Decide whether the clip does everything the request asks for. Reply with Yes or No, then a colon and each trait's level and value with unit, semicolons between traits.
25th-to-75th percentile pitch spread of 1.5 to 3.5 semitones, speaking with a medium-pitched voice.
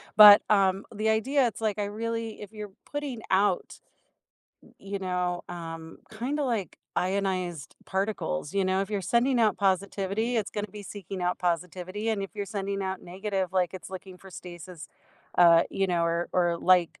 No: average, 2.8 semitones; high, 195 Hz